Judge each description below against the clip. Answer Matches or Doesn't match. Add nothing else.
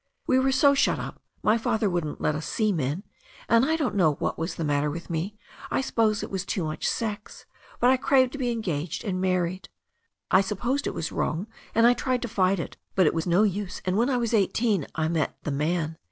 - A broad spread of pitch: Matches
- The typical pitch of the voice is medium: Doesn't match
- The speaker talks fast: Matches